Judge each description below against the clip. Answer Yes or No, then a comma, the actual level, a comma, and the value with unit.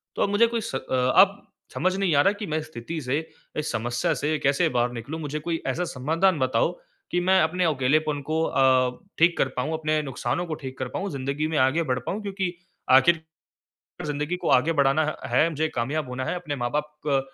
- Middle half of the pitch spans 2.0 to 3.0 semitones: No, average, 4.2 semitones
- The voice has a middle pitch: Yes, medium, 150 Hz